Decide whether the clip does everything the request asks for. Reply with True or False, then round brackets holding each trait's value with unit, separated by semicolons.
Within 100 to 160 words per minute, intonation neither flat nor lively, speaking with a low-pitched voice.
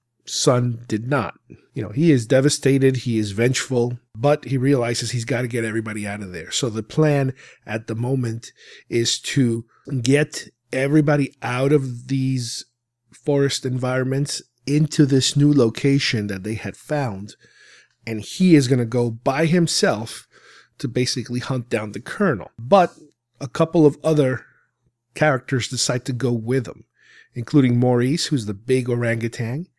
True (155 wpm; 3.3 semitones; 130 Hz)